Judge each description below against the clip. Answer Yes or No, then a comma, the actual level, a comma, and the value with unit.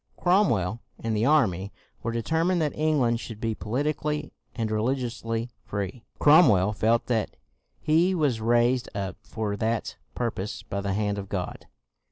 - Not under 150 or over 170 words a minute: Yes, average, 155 wpm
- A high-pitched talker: No, low, 115 Hz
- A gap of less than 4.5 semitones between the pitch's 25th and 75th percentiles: No, wide, 5.6 semitones